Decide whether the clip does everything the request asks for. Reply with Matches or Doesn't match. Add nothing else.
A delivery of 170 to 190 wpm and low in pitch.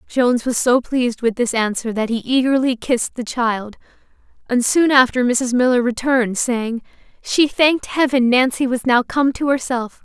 Doesn't match